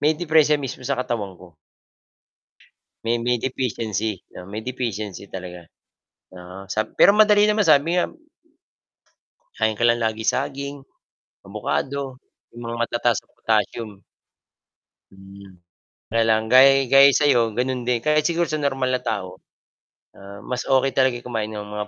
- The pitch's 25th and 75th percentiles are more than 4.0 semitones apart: Yes, average, 4.4 semitones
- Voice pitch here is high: No, low, 120 Hz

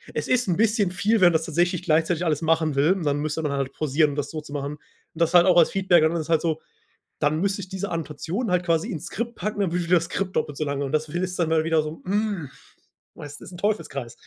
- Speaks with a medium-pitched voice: Yes, medium, 165 Hz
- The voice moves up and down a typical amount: Yes, average, 3.2 semitones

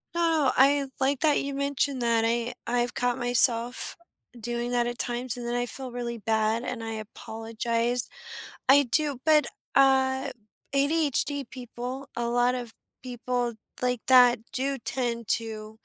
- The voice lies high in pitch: Yes, high, 245 Hz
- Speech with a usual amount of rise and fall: No, narrow, 2.2 semitones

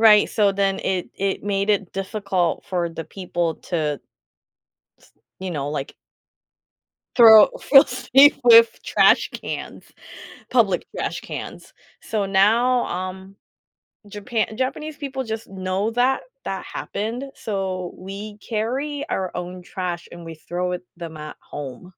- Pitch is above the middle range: Yes, high, 195 Hz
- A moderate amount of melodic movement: Yes, average, 3.9 semitones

